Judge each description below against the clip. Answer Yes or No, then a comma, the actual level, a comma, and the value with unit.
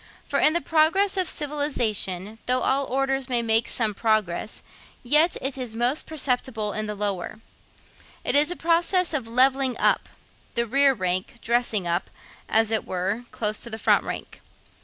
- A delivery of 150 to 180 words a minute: Yes, average, 165 wpm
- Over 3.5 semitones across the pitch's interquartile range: Yes, average, 4.6 semitones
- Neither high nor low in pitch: No, high, 240 Hz